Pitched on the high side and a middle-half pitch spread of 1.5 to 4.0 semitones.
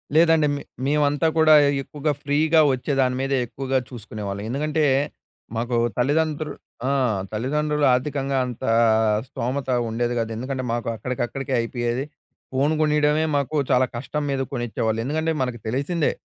No: low, 135 Hz; average, 3.6 semitones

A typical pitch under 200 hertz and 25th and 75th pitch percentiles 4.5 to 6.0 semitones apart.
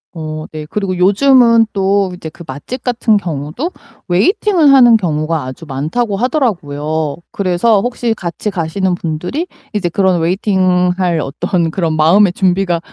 Yes: medium, 185 Hz; average, 5.1 semitones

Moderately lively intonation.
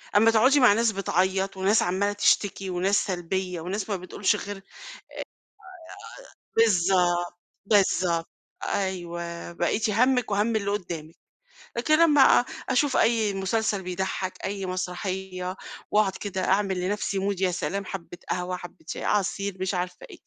No: narrow, 2.3 semitones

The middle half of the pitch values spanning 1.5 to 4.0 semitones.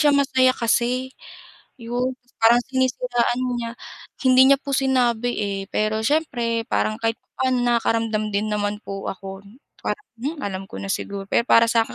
Yes: average, 3.2 semitones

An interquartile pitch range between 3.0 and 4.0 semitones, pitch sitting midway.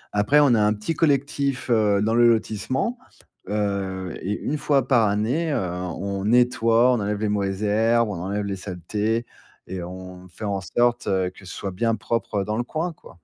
No: average, 3.7 semitones; low, 105 Hz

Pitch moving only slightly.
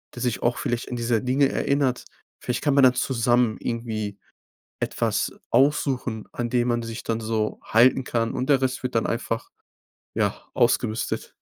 Yes: narrow, 2.1 semitones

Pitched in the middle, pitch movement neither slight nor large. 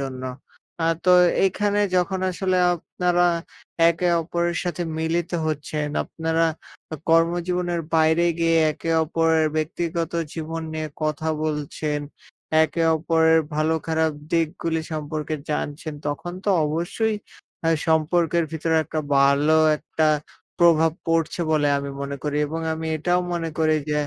No: medium, 160 Hz; narrow, 1.8 semitones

